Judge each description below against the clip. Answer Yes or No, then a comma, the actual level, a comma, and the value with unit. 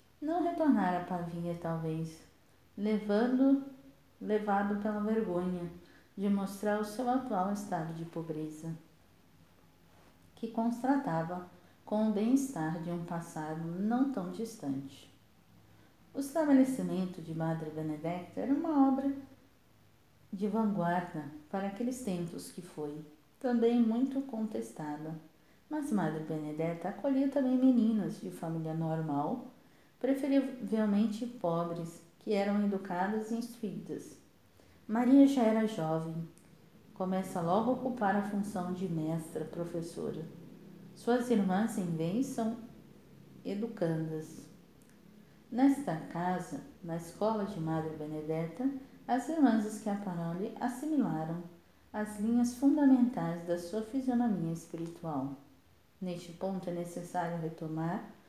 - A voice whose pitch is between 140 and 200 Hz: Yes, high, 190 Hz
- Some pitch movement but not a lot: No, wide, 5.9 semitones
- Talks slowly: Yes, slow, 110 wpm